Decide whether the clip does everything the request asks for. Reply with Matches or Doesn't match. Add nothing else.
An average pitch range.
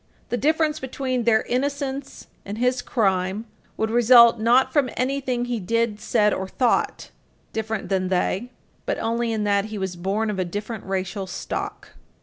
Matches